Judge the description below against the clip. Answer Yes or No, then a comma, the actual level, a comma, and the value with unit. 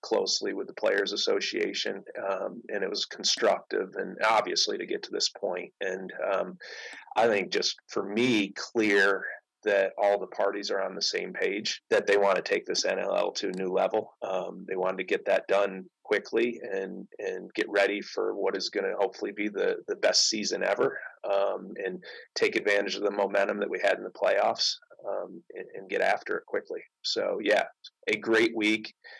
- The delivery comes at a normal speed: Yes, average, 195 wpm